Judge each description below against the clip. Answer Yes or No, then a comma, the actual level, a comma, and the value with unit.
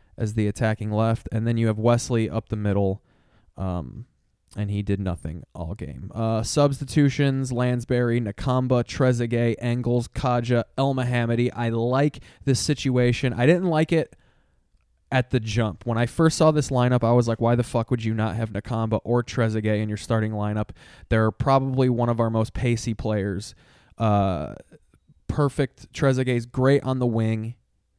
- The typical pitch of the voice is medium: No, low, 120 Hz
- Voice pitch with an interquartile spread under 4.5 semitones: Yes, average, 2.8 semitones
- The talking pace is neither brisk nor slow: Yes, average, 165 wpm